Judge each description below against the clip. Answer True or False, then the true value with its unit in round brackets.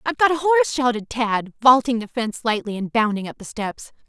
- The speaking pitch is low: False (240 Hz)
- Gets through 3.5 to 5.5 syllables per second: False (5.9 syllables/s)